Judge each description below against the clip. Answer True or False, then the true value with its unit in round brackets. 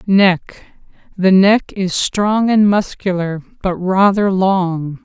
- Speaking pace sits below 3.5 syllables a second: True (3.1 syllables/s)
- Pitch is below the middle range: False (190 Hz)